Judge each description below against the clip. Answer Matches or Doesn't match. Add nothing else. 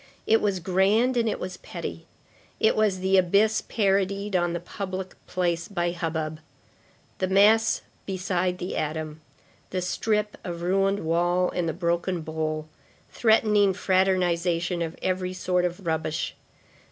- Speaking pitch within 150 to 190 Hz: Matches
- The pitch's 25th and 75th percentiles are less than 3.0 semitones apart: Matches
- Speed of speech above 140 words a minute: Doesn't match